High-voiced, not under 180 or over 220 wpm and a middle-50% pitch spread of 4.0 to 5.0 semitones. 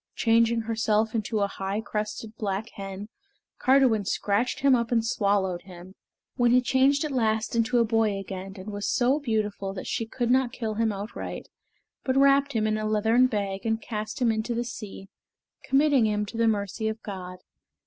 No: high, 220 Hz; average, 185 wpm; average, 2.9 semitones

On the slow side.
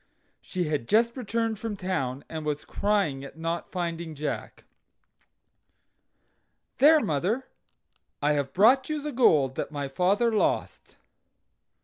Yes: slow, 125 wpm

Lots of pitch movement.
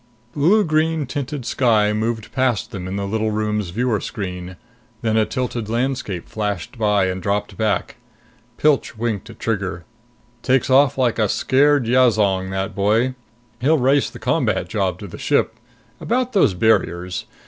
No: average, 4.6 semitones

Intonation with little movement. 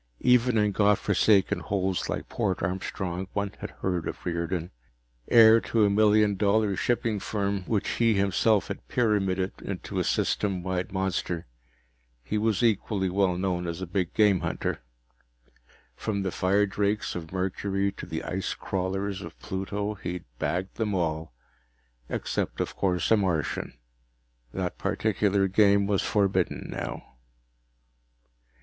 Yes: narrow, 2.1 semitones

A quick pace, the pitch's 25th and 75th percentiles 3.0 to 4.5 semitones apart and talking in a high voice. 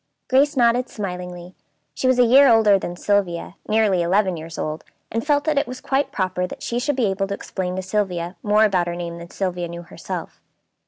No: fast, 210 wpm; average, 5.0 semitones; high, 195 Hz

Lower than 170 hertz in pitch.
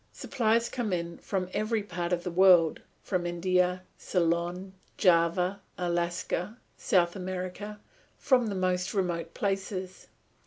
No: medium, 185 Hz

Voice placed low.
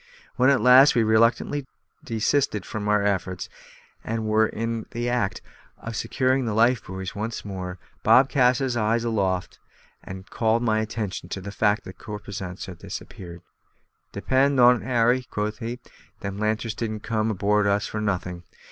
Yes: low, 110 Hz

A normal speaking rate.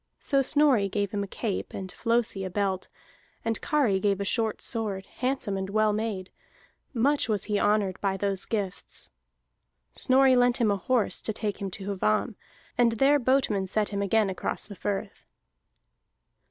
Yes: average, 165 wpm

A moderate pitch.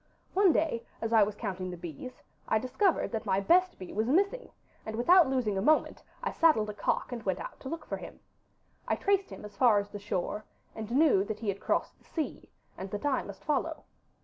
No: high, 230 Hz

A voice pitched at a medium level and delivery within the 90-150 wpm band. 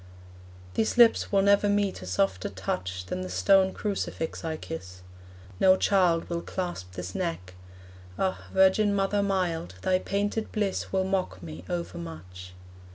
Yes: medium, 170 Hz; average, 145 wpm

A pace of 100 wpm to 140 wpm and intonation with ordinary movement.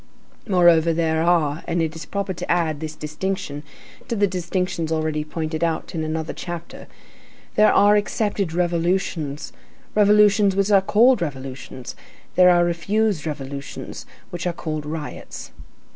Yes: slow, 135 wpm; average, 3.5 semitones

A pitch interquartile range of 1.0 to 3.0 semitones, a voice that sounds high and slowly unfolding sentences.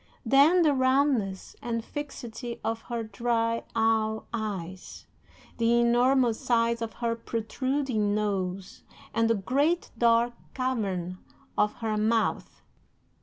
Yes: narrow, 2.5 semitones; high, 230 Hz; slow, 115 wpm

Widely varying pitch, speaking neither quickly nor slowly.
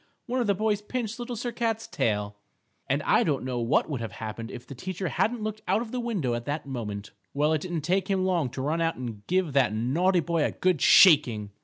No: wide, 8.7 semitones; fast, 235 wpm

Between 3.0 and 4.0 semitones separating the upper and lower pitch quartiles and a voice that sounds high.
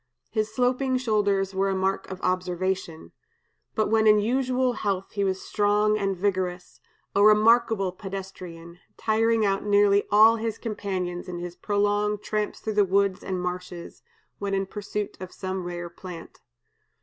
No: narrow, 2.4 semitones; high, 200 Hz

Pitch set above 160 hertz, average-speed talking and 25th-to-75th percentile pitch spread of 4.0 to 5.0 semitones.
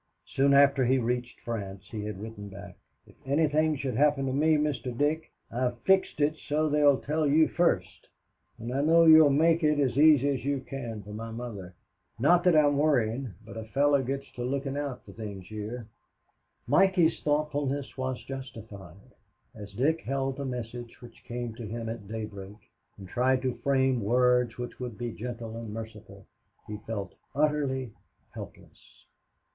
No: low, 130 Hz; average, 170 wpm; average, 4.3 semitones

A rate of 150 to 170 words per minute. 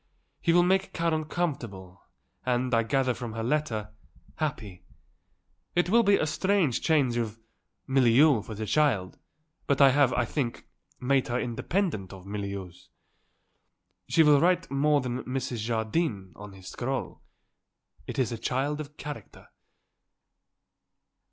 No: average, 140 wpm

